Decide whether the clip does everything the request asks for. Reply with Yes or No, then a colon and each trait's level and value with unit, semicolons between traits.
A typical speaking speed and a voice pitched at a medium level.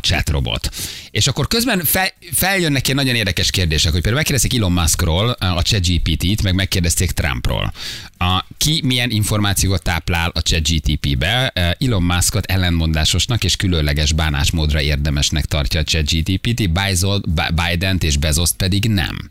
No: average, 145 wpm; very low, 90 Hz